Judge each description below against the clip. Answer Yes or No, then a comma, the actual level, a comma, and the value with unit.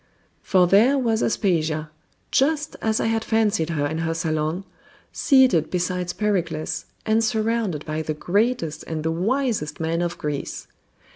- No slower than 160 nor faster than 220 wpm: No, average, 145 wpm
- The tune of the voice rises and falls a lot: Yes, wide, 5.9 semitones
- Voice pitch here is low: No, medium, 180 Hz